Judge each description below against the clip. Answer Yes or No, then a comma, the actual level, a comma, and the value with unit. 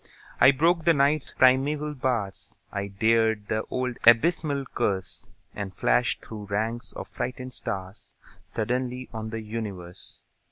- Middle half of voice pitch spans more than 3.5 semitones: Yes, average, 4.0 semitones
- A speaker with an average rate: No, slow, 130 wpm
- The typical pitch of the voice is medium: No, low, 115 Hz